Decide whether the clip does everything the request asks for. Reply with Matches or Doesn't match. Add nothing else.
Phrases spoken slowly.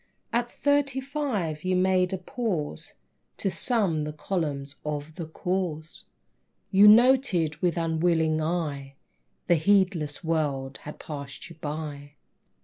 Matches